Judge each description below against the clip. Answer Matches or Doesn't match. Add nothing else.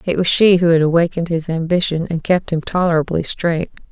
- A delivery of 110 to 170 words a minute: Doesn't match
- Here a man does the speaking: Doesn't match